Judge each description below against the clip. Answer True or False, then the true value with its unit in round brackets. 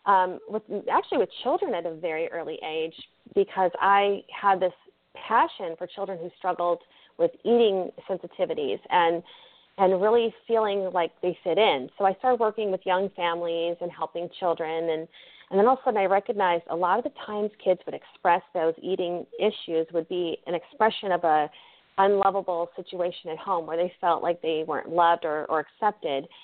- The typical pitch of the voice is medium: True (180 Hz)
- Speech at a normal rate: True (180 wpm)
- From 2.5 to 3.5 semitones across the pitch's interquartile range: True (2.9 semitones)